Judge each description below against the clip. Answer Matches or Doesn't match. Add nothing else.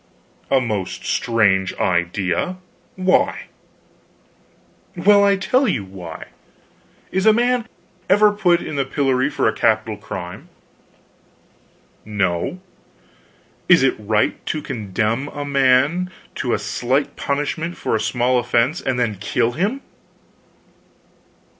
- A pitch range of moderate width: Doesn't match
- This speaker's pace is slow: Matches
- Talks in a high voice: Doesn't match